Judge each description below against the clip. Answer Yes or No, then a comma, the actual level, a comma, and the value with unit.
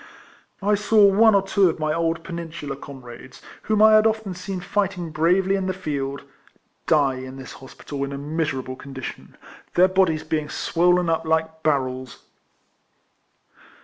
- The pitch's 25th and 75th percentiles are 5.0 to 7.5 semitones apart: Yes, wide, 5.4 semitones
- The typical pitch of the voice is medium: Yes, medium, 165 Hz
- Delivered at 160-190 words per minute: No, average, 150 wpm